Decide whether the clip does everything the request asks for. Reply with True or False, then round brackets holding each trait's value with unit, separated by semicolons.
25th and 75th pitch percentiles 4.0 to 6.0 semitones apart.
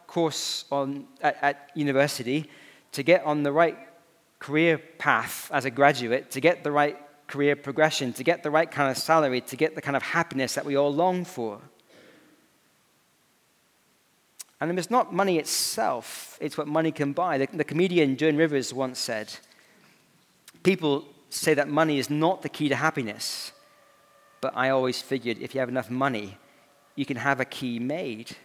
False (2.9 semitones)